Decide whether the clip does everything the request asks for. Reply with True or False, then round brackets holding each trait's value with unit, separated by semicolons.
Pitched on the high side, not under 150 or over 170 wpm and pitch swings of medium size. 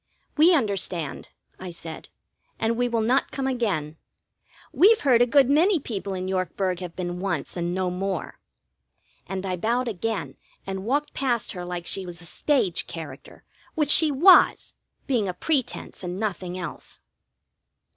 False (195 Hz; 155 wpm; 6.2 semitones)